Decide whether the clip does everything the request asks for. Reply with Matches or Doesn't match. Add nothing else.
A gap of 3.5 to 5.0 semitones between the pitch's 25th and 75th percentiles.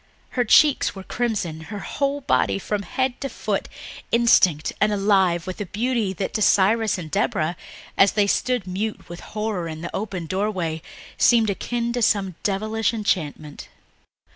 Matches